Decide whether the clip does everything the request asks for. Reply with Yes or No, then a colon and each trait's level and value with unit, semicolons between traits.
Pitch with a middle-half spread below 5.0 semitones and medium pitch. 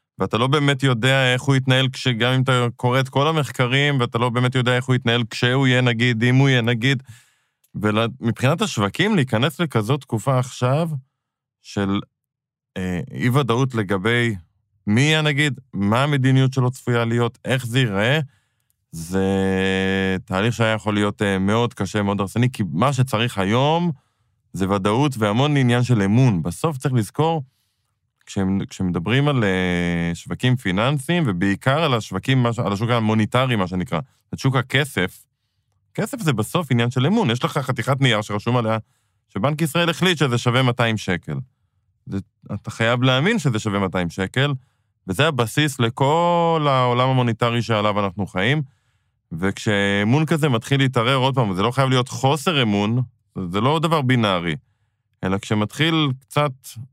No: average, 4.4 semitones; low, 120 Hz